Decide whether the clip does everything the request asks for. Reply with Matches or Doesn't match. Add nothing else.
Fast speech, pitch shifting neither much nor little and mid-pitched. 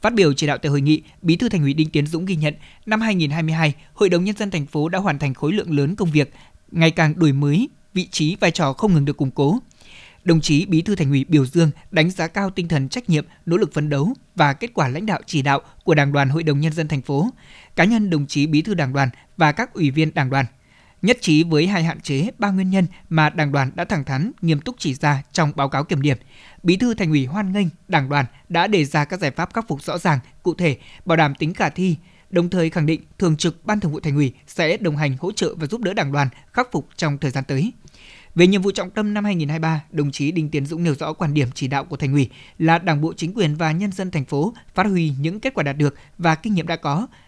Matches